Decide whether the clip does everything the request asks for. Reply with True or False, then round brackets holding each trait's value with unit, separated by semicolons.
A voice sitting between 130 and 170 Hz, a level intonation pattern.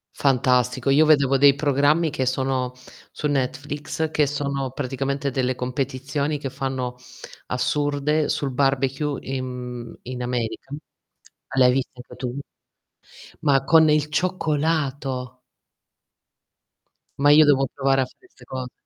True (135 Hz; 2.2 semitones)